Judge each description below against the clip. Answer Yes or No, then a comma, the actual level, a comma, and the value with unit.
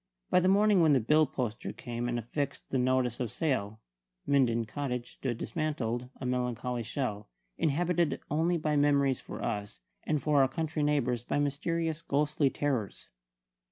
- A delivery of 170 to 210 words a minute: No, average, 155 wpm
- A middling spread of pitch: Yes, average, 4.0 semitones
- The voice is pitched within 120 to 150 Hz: Yes, medium, 140 Hz